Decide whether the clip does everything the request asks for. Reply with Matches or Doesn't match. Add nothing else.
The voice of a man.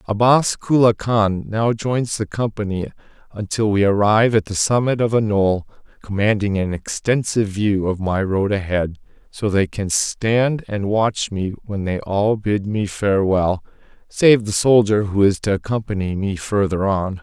Matches